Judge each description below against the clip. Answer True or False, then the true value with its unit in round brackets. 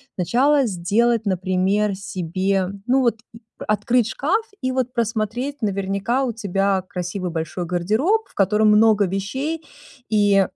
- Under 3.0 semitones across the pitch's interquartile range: False (4.3 semitones)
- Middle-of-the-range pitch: False (210 Hz)